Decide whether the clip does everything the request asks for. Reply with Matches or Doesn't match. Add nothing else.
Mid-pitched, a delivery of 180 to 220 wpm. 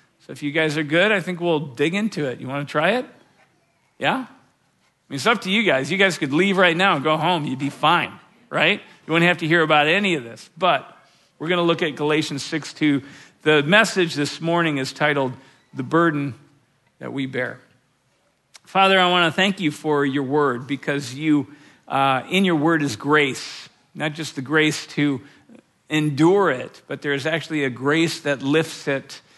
Matches